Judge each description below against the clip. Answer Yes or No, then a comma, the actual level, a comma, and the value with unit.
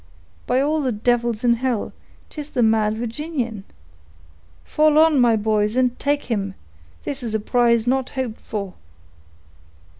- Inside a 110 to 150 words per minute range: Yes, average, 140 wpm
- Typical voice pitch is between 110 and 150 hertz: No, high, 235 Hz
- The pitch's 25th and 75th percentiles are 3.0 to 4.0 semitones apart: Yes, average, 3.7 semitones